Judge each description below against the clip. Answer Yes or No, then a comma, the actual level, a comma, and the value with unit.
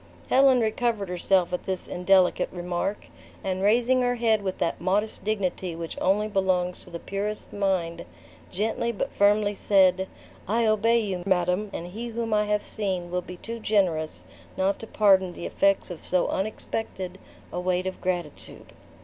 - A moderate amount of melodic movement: Yes, average, 3.0 semitones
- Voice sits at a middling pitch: No, high, 195 Hz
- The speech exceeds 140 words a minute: Yes, average, 165 wpm